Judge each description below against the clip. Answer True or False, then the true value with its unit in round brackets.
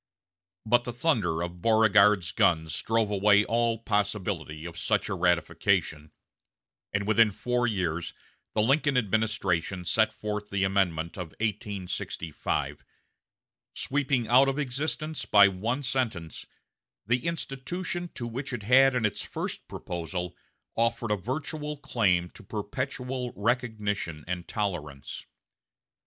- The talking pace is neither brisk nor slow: False (120 wpm)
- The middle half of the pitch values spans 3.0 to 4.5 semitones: False (5.3 semitones)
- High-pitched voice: False (105 Hz)